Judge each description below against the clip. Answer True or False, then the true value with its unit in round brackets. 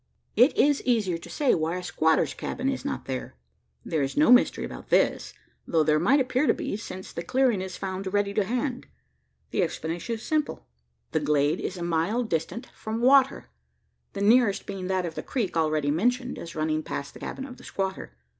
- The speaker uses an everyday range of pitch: False (7.3 semitones)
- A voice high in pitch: True (195 Hz)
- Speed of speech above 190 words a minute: True (200 wpm)